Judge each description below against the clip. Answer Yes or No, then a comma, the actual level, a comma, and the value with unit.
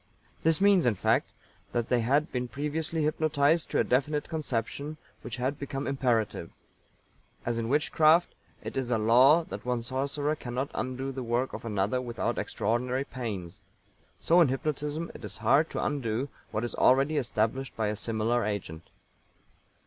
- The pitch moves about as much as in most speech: Yes, average, 4.1 semitones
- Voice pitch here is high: No, low, 130 Hz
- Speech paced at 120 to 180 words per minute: Yes, average, 160 wpm